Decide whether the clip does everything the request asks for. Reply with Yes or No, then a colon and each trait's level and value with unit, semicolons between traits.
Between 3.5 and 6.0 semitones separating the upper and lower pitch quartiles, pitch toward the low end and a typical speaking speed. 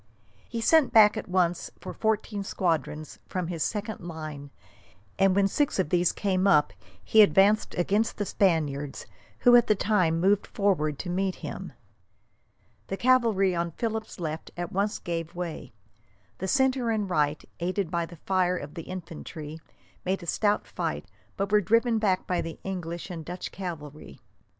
No: average, 3.8 semitones; medium, 185 Hz; average, 165 wpm